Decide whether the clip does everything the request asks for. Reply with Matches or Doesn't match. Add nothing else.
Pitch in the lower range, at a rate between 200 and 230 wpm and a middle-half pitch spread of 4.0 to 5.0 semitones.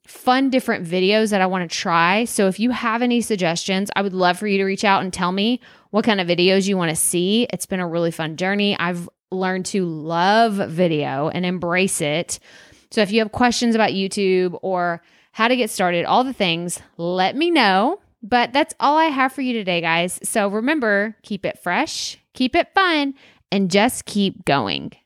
Doesn't match